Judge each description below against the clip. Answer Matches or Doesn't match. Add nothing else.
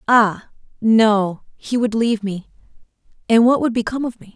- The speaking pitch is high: Matches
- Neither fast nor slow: Matches